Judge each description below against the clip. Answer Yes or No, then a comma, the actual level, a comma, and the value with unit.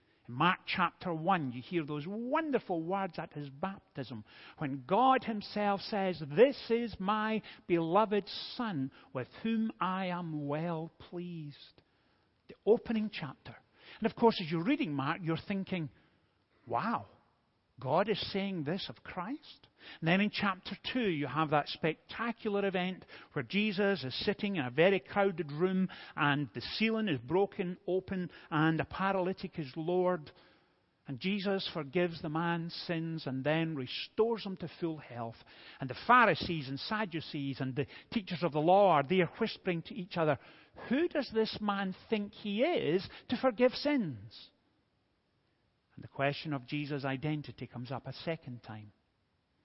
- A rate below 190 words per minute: Yes, average, 150 wpm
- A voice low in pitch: No, medium, 175 Hz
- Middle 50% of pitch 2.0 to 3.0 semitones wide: No, wide, 5.5 semitones